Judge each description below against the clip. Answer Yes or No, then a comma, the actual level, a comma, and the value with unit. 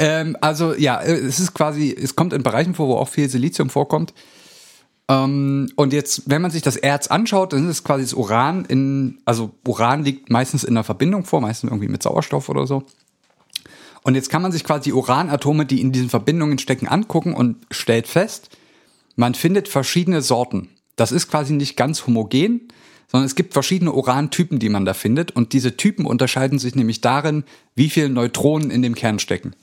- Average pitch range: Yes, average, 3.7 semitones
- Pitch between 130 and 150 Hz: Yes, medium, 140 Hz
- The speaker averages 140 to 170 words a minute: No, fast, 190 wpm